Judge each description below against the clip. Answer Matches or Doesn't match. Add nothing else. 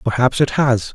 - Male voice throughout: Matches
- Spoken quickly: Doesn't match